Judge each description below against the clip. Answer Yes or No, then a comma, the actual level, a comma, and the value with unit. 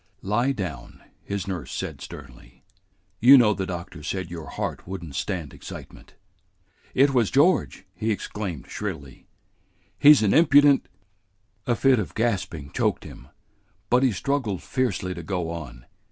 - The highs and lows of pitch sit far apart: Yes, wide, 6.6 semitones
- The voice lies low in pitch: Yes, low, 100 Hz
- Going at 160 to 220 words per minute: No, average, 150 wpm